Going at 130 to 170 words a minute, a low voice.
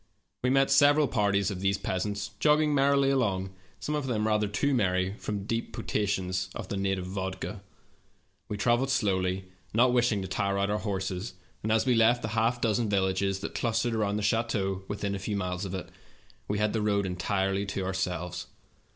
No: average, 185 wpm; low, 105 Hz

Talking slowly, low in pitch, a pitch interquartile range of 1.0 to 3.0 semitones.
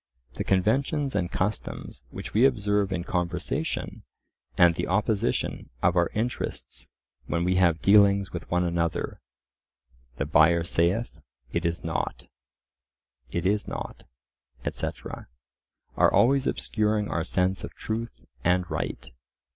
No: slow, 125 wpm; very low, 90 Hz; average, 3.8 semitones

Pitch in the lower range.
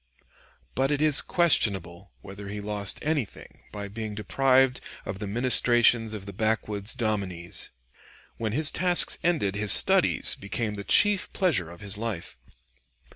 Yes: low, 110 Hz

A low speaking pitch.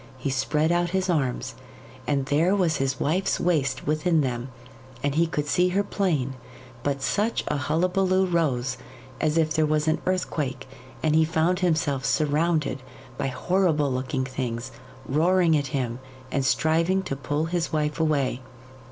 No: medium, 155 Hz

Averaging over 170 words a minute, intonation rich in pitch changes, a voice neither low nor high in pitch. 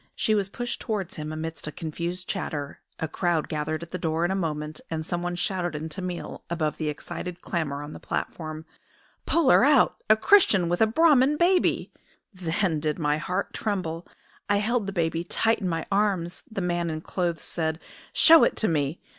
No: average, 190 wpm; average, 4.0 semitones; medium, 175 Hz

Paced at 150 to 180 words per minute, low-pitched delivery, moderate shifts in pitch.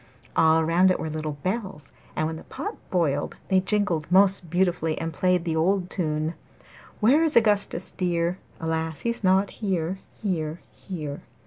No: average, 155 wpm; medium, 175 Hz; average, 3.1 semitones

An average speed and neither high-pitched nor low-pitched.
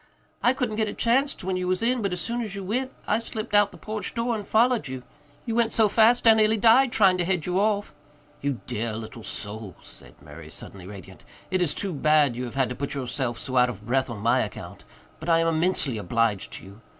No: fast, 245 wpm; medium, 180 Hz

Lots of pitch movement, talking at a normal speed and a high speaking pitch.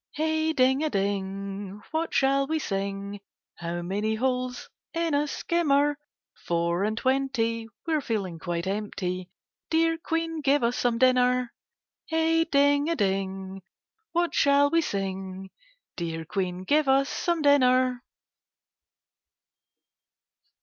No: wide, 7.0 semitones; slow, 120 wpm; very high, 250 Hz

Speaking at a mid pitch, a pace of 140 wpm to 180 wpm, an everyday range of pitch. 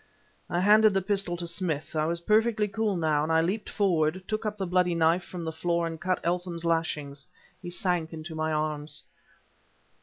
No: medium, 170 Hz; average, 190 wpm; average, 3.0 semitones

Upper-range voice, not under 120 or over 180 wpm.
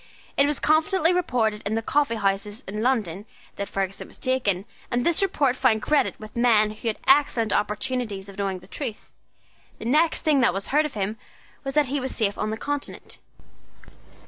No: high, 230 Hz; average, 190 wpm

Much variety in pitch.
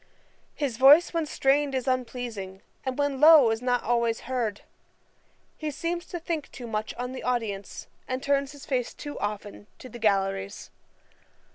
No: average, 4.2 semitones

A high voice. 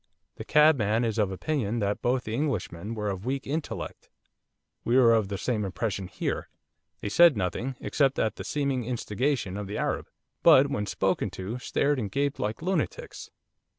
No: low, 115 Hz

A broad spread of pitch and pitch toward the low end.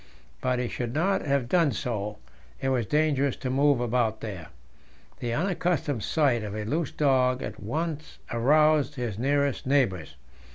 No: average, 4.1 semitones; low, 130 Hz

